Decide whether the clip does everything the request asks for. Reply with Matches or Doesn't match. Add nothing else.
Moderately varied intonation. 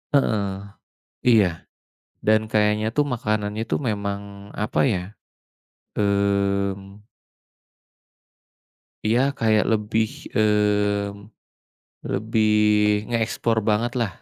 Doesn't match